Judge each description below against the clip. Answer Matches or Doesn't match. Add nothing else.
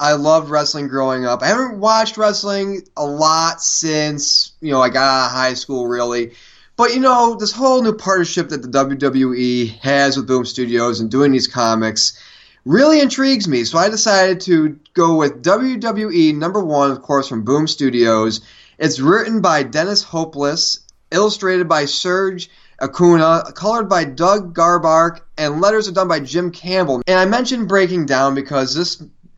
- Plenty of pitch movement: Matches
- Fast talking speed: Doesn't match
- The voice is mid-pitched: Matches